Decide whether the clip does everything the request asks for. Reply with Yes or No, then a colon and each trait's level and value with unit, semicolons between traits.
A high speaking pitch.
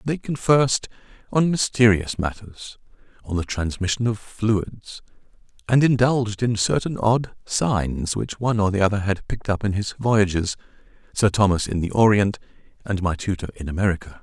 No: low, 105 Hz